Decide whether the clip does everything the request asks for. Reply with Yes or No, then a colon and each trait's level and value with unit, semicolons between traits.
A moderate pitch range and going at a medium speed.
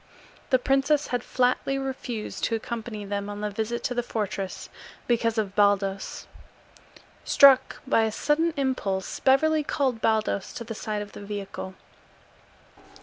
Yes: average, 4.3 semitones; average, 145 wpm